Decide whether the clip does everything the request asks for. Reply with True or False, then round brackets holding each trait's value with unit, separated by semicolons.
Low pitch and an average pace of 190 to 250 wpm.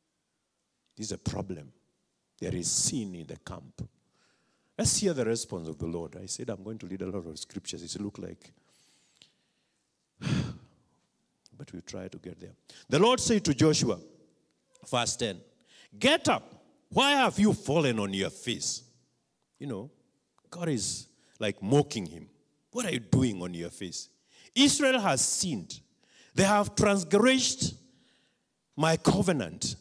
False (130 Hz; 150 wpm)